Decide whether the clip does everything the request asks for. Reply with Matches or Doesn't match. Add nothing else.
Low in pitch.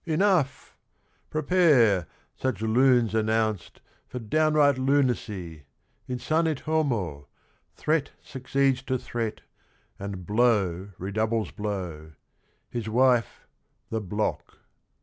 Matches